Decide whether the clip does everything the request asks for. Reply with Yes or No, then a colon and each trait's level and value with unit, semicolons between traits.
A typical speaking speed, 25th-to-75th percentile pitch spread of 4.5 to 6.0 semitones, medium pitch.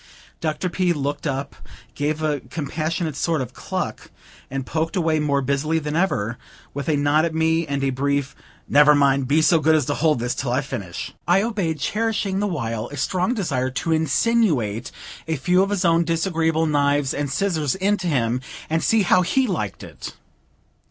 No: average, 185 wpm; average, 3.6 semitones; medium, 155 Hz